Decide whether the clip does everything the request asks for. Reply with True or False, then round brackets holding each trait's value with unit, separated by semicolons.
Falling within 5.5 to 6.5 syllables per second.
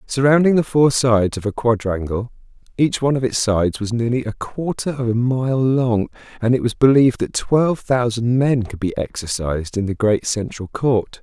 False (5.1 syllables/s)